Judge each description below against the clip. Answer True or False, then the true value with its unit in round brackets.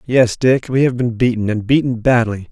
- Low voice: True (120 Hz)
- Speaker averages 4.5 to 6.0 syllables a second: True (5.0 syllables/s)